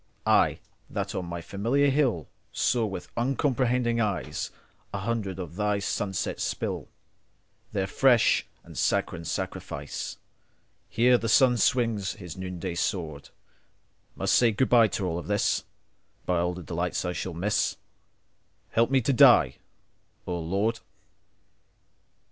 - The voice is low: Yes, low, 100 Hz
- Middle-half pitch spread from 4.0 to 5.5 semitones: Yes, average, 4.7 semitones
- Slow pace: Yes, slow, 115 wpm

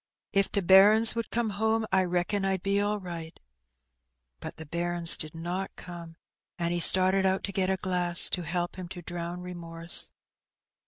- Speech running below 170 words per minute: No, average, 175 wpm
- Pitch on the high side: No, medium, 180 Hz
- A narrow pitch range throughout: Yes, narrow, 2.1 semitones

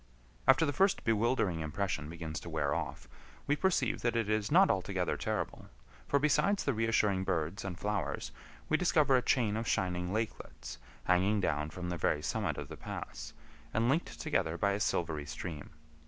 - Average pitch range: No, wide, 6.0 semitones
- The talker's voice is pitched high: No, low, 100 Hz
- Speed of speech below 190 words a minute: Yes, average, 175 wpm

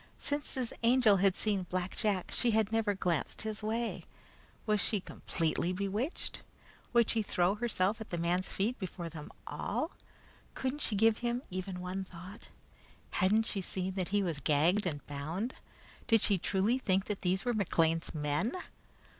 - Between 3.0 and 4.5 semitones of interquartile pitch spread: Yes, average, 3.7 semitones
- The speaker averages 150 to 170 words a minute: Yes, average, 165 wpm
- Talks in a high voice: Yes, high, 195 Hz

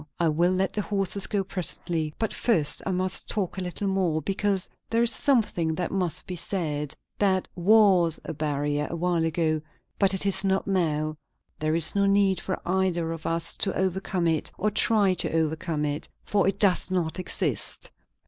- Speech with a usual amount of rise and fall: Yes, average, 3.3 semitones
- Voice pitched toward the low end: No, medium, 180 Hz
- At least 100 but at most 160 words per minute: No, average, 185 wpm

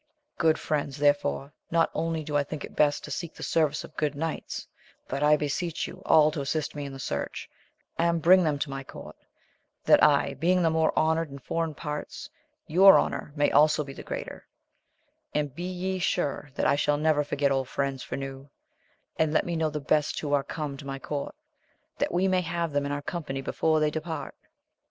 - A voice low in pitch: No, medium, 150 Hz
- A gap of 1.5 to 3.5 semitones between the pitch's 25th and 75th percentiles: Yes, narrow, 2.4 semitones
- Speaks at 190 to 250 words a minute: Yes, fast, 205 wpm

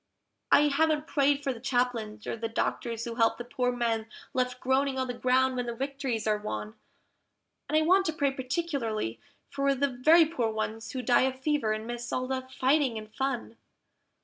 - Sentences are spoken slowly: No, average, 195 wpm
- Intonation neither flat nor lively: Yes, average, 3.3 semitones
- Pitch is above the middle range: Yes, very high, 255 Hz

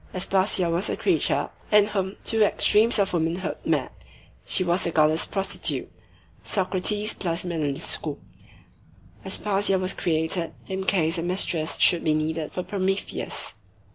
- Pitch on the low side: No, medium, 185 Hz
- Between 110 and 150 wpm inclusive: Yes, average, 140 wpm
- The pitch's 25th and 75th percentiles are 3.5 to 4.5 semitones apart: No, average, 2.8 semitones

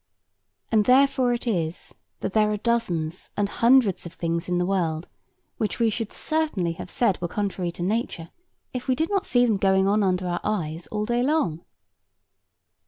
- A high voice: Yes, high, 205 Hz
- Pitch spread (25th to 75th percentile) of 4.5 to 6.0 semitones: Yes, average, 5.2 semitones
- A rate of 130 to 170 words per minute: No, average, 180 wpm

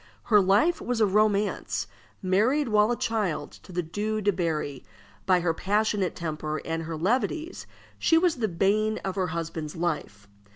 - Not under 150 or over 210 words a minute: Yes, average, 165 wpm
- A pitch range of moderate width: Yes, average, 4.6 semitones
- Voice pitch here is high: Yes, high, 195 Hz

